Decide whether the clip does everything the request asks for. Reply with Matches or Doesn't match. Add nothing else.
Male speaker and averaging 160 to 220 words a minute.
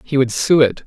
Doesn't match